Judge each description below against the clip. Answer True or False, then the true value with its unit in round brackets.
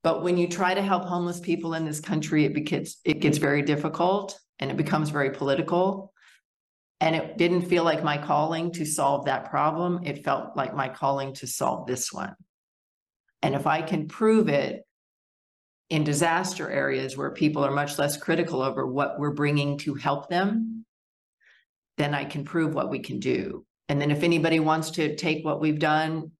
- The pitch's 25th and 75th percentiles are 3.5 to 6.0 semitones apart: False (2.9 semitones)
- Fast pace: False (185 wpm)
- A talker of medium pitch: True (155 Hz)